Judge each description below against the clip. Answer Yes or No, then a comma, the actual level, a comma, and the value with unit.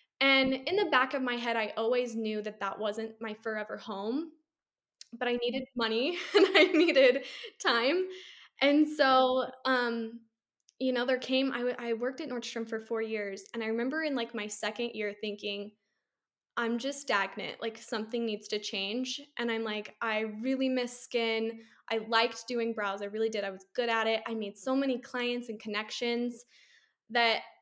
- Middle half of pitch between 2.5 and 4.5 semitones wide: Yes, average, 2.8 semitones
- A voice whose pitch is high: Yes, high, 235 Hz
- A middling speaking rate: Yes, average, 185 wpm